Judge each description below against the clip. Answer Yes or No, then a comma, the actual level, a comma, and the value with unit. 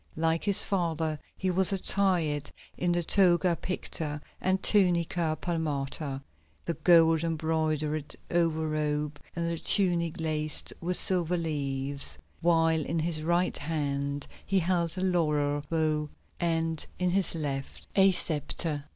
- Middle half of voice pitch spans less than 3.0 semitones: Yes, narrow, 2.5 semitones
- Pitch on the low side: No, medium, 165 Hz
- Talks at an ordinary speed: No, slow, 130 wpm